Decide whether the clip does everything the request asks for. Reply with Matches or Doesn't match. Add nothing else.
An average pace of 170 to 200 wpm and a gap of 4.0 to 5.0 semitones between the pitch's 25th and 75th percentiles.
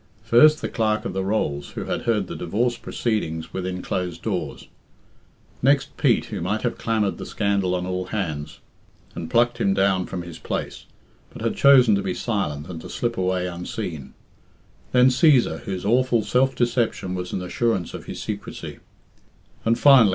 Matches